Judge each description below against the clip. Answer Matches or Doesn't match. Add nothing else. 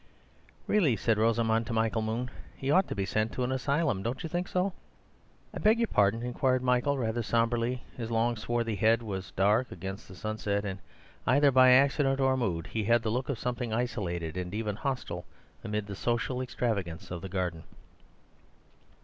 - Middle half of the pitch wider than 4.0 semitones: Doesn't match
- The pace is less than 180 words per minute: Doesn't match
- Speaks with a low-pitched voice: Matches